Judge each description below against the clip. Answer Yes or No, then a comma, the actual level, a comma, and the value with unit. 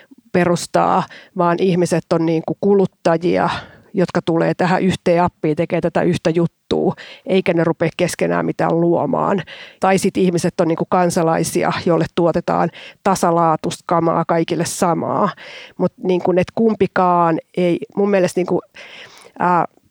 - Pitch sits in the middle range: Yes, medium, 175 Hz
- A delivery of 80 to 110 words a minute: No, average, 125 wpm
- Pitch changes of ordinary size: No, narrow, 1.6 semitones